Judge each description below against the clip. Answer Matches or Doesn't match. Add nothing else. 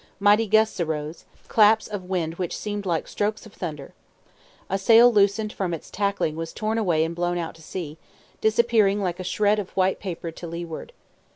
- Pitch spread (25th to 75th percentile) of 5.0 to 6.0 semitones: Doesn't match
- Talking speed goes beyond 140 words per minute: Matches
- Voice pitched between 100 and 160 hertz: Doesn't match